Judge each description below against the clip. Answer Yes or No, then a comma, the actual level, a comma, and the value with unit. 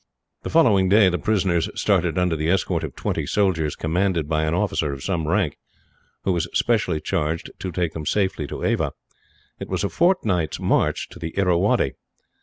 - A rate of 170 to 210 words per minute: Yes, average, 180 wpm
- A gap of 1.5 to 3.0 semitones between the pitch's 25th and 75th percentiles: No, average, 3.6 semitones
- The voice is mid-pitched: No, very low, 90 Hz